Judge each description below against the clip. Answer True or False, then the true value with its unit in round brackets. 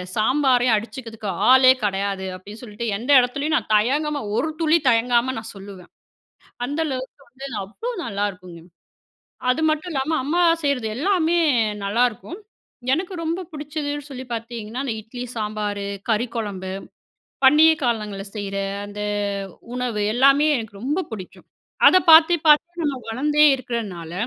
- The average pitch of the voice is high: True (245 Hz)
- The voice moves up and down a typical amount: False (5.8 semitones)